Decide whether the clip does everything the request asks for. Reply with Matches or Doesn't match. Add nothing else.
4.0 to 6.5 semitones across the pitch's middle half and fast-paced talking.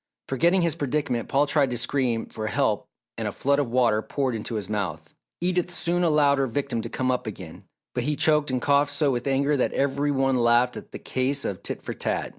Doesn't match